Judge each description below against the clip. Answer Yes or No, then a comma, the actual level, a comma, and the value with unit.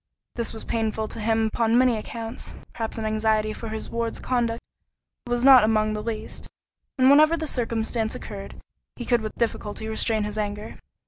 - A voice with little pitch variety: Yes, narrow, 1.6 semitones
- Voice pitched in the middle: No, high, 225 Hz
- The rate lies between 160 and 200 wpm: Yes, average, 175 wpm